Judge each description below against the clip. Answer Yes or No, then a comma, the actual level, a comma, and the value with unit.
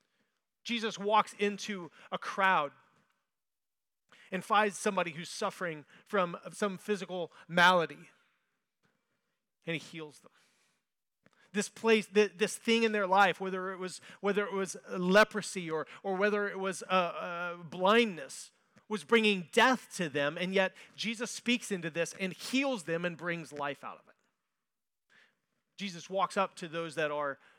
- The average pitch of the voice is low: No, high, 190 Hz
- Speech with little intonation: No, average, 3.2 semitones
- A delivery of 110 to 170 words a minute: Yes, average, 145 wpm